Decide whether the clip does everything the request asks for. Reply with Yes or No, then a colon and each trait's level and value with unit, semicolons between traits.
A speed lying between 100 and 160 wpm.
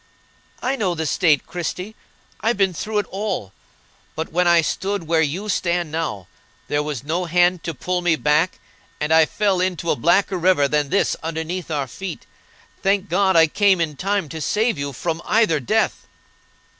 No: average, 180 wpm